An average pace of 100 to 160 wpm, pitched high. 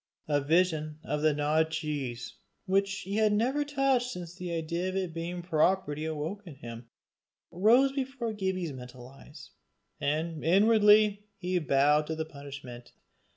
No: average, 150 wpm; medium, 170 Hz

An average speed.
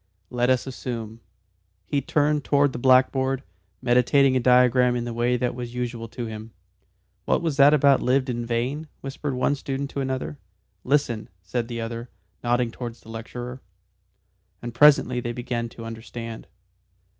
Yes: average, 160 wpm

